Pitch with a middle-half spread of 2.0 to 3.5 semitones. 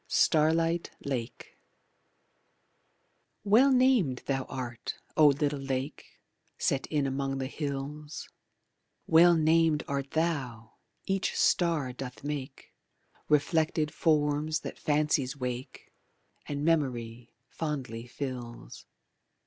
Yes: average, 3.2 semitones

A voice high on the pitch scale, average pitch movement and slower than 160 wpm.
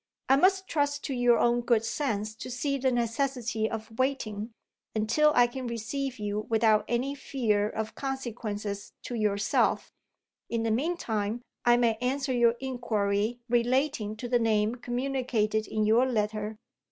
Yes: high, 235 Hz; average, 3.2 semitones; average, 150 wpm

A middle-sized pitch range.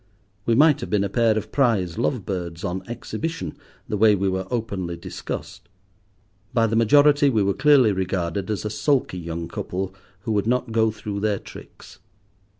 Yes: average, 4.1 semitones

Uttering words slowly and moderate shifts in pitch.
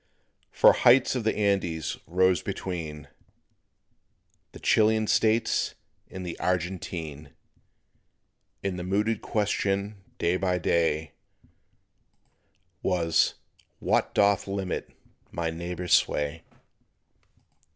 Yes: slow, 90 wpm; average, 3.4 semitones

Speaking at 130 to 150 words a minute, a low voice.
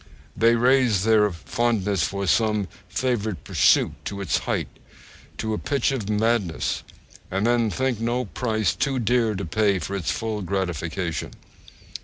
Yes: average, 140 wpm; low, 110 Hz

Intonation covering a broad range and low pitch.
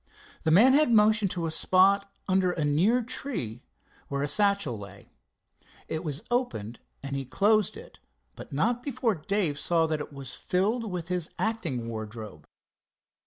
No: wide, 7.4 semitones; medium, 180 Hz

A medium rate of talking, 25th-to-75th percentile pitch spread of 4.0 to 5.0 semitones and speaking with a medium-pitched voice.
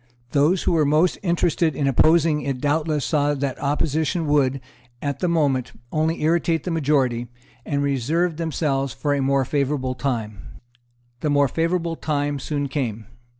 No: average, 150 wpm; average, 2.8 semitones; medium, 145 Hz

